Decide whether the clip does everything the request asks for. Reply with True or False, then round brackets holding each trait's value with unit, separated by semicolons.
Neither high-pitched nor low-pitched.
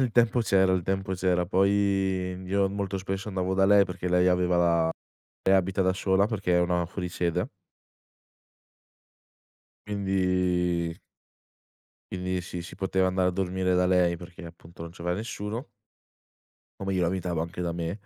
False (90 Hz)